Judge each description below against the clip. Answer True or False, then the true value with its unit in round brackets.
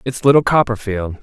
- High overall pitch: False (120 Hz)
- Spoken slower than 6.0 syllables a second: True (5.4 syllables/s)